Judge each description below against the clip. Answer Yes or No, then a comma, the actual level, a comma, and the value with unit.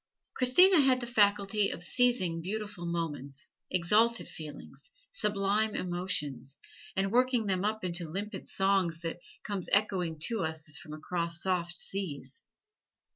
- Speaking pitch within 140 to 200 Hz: Yes, high, 190 Hz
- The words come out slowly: Yes, slow, 130 wpm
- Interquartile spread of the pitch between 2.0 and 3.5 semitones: No, average, 4.1 semitones